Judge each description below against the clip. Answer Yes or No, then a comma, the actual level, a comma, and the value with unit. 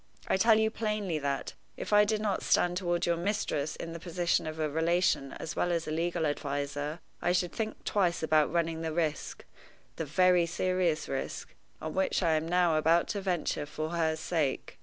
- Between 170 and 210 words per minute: Yes, average, 195 wpm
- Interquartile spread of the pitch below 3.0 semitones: Yes, narrow, 2.6 semitones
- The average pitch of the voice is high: No, medium, 170 Hz